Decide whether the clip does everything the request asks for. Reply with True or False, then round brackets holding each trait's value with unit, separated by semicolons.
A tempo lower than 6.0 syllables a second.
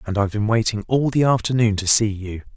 False (6.1 syllables/s)